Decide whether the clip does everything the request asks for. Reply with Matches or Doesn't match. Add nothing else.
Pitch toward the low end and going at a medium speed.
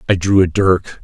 Doesn't match